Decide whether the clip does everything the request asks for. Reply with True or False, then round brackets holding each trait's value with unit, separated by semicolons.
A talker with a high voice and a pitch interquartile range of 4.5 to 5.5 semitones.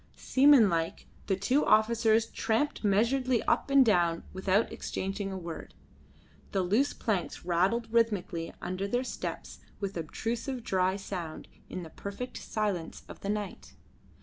False (200 Hz; 4.0 semitones)